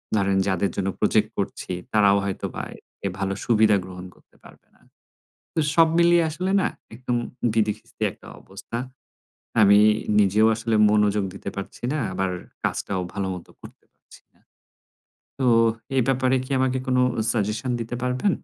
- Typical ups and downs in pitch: Yes, average, 4.4 semitones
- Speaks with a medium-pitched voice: No, low, 105 Hz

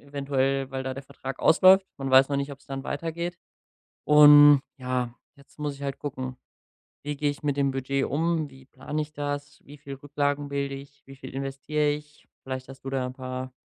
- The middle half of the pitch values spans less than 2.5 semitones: Yes, narrow, 1.6 semitones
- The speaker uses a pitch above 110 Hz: Yes, medium, 140 Hz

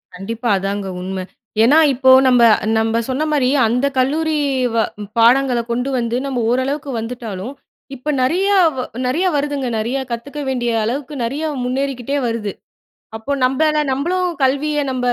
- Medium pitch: No, very high, 260 Hz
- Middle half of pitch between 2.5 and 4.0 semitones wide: Yes, average, 3.4 semitones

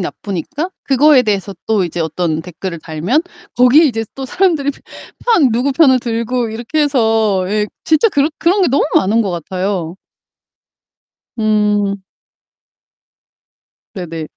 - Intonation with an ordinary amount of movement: No, wide, 6.6 semitones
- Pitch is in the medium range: No, high, 225 Hz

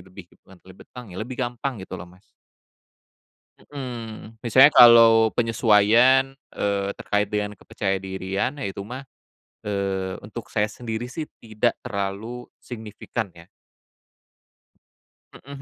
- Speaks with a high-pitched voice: No, low, 110 Hz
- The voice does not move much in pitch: No, average, 3.7 semitones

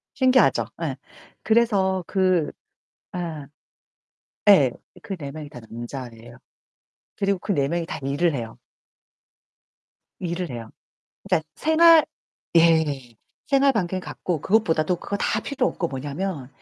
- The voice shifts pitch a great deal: Yes, wide, 6.1 semitones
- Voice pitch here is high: No, medium, 170 Hz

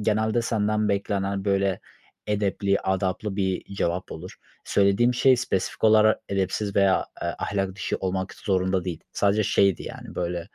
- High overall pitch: No, low, 100 Hz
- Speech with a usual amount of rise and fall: No, narrow, 2.0 semitones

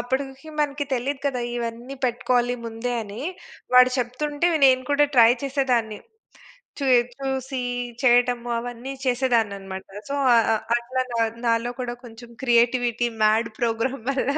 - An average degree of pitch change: No, narrow, 2.2 semitones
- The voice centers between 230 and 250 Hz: Yes, high, 245 Hz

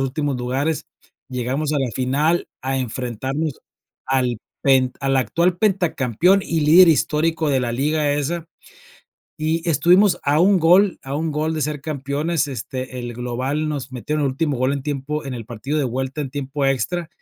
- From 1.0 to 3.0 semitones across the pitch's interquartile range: No, average, 3.4 semitones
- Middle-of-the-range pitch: Yes, medium, 145 Hz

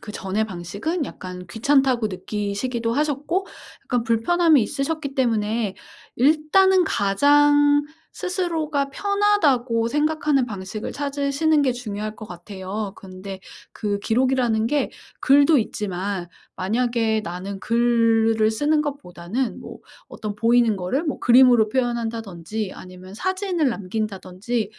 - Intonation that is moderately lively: No, wide, 5.8 semitones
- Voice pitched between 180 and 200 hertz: No, high, 235 Hz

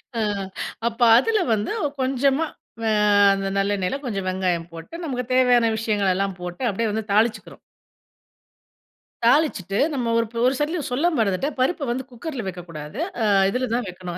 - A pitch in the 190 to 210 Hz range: No, high, 225 Hz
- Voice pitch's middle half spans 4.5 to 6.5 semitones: Yes, average, 5.3 semitones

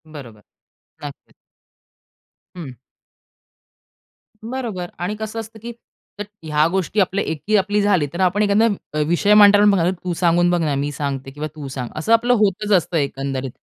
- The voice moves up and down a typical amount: No, wide, 6.0 semitones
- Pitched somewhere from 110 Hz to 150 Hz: No, medium, 180 Hz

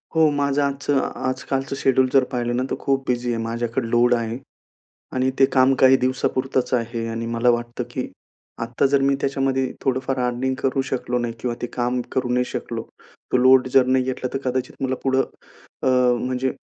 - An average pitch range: No, narrow, 1.5 semitones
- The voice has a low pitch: Yes, low, 130 Hz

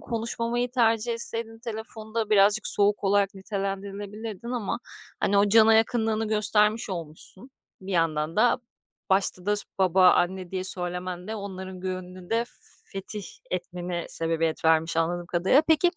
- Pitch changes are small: No, average, 3.4 semitones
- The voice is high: Yes, high, 200 Hz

